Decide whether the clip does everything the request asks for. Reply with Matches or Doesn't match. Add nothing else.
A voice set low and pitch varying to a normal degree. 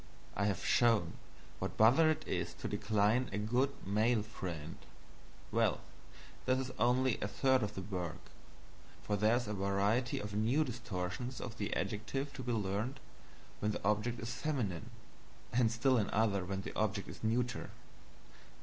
Matches